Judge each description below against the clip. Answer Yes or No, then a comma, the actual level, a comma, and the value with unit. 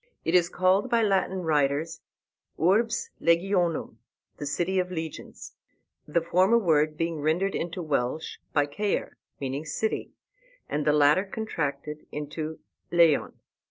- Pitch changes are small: No, average, 3.7 semitones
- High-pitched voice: No, medium, 165 Hz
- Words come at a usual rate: No, slow, 125 wpm